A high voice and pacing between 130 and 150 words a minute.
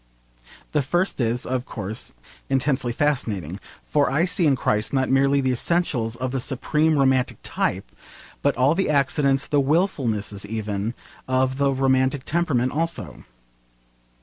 No: low, 135 Hz; average, 140 wpm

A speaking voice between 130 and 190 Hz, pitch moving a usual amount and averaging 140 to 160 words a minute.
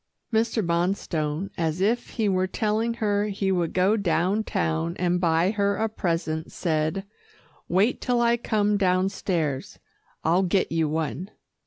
Yes: medium, 185 Hz; average, 4.1 semitones; average, 145 wpm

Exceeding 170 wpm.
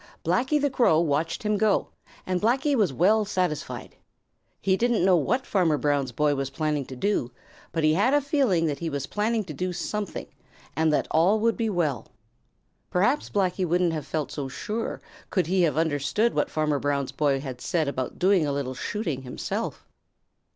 Yes: average, 185 wpm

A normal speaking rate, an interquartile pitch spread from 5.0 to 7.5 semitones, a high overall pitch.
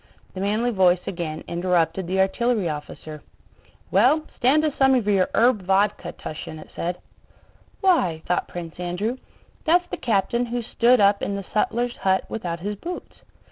Yes: average, 160 wpm; average, 5.3 semitones; high, 200 Hz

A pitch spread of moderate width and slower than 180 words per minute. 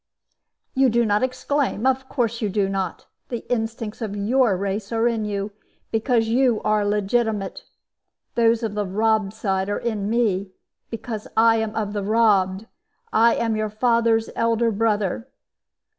No: narrow, 2.2 semitones; average, 155 wpm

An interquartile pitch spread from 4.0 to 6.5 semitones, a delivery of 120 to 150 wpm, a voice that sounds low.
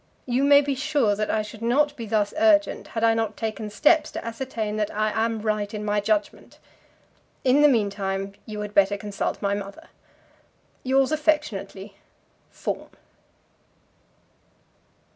No: average, 4.7 semitones; average, 145 wpm; high, 220 Hz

